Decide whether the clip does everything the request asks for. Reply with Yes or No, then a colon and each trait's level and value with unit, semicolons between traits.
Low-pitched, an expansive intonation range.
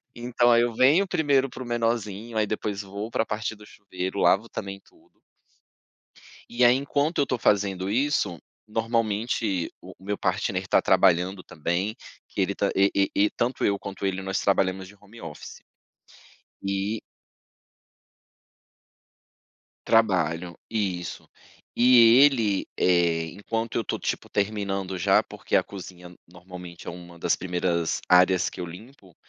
No: low, 100 Hz; average, 3.8 semitones